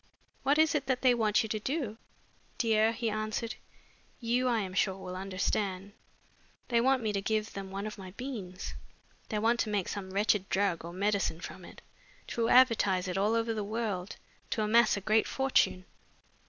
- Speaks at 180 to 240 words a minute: Yes, average, 185 wpm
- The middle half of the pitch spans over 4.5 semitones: No, average, 3.2 semitones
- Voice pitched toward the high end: Yes, high, 215 Hz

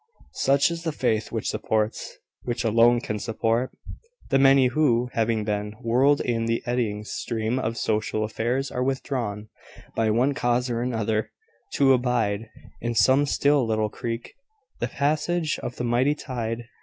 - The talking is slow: No, average, 155 wpm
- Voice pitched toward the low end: Yes, low, 120 Hz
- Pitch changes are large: No, average, 3.0 semitones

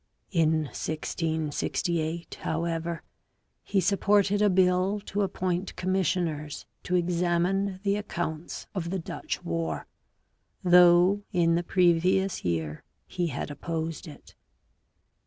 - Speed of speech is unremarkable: No, slow, 105 wpm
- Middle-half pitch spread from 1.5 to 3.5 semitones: Yes, average, 2.7 semitones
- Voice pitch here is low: No, medium, 175 Hz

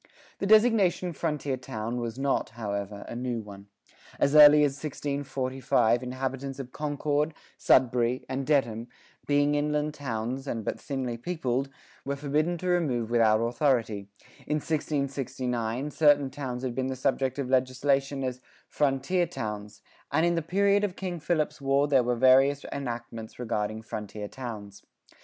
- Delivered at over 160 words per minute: No, average, 145 wpm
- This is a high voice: No, low, 135 Hz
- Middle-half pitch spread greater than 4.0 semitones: No, average, 3.6 semitones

